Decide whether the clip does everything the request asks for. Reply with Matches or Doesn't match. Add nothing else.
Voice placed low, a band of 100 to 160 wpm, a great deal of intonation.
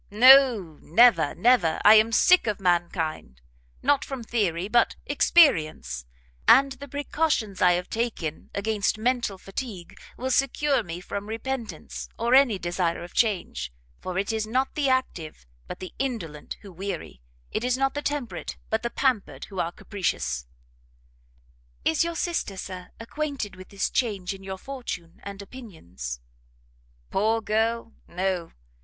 Doesn't match